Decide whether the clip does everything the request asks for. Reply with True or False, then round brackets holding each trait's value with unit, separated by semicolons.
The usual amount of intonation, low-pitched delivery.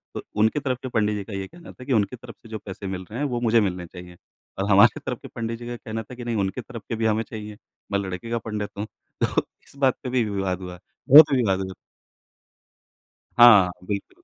True (3.7 semitones; 110 Hz)